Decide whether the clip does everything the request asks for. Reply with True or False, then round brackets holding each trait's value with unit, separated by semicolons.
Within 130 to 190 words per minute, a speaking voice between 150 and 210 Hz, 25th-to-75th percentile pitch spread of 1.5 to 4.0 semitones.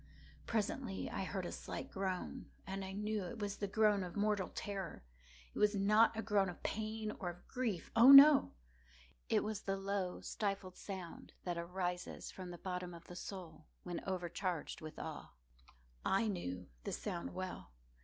True (165 wpm; 190 Hz; 2.9 semitones)